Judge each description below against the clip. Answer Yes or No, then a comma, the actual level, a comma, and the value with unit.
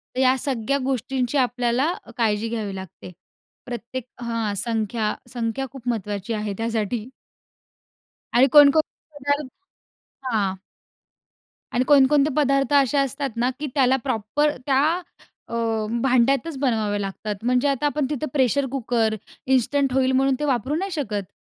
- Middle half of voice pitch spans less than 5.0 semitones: Yes, average, 3.5 semitones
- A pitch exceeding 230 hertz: Yes, very high, 255 Hz